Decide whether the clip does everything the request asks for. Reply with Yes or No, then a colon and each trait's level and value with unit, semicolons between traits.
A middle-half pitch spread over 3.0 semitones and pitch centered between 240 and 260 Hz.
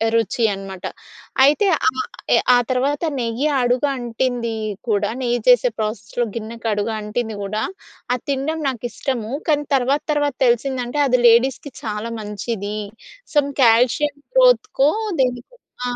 Yes: average, 3.7 semitones; high, 245 Hz